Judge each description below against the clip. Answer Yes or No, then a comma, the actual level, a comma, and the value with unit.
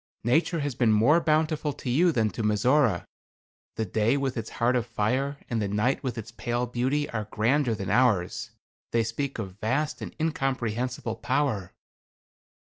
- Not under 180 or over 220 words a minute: No, average, 165 wpm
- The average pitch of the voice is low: Yes, low, 120 Hz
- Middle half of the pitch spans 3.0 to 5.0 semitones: Yes, average, 4.1 semitones